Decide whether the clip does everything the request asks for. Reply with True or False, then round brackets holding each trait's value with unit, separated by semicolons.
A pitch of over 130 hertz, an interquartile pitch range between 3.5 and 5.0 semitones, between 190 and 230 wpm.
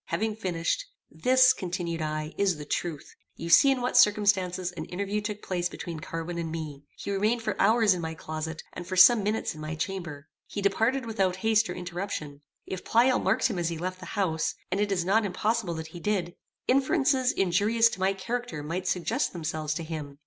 True (185 Hz; 4.6 semitones; 200 wpm)